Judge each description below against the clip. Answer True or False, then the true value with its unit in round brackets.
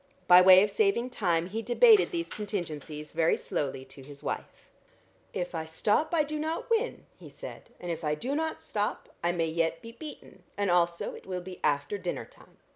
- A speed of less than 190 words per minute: False (200 wpm)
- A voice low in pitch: False (185 Hz)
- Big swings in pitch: True (7.3 semitones)